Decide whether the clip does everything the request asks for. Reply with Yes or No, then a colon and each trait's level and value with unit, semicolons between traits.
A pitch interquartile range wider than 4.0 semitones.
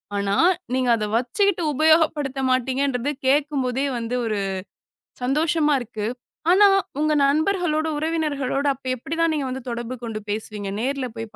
Yes: average, 4.4 semitones